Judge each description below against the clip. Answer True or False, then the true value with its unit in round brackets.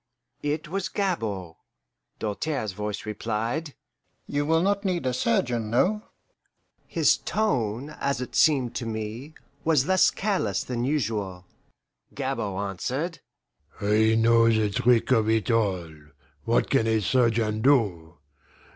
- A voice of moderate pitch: False (115 Hz)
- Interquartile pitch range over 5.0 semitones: True (5.5 semitones)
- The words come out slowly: True (125 wpm)